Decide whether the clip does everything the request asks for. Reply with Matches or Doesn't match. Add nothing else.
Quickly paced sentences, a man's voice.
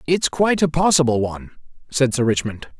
Doesn't match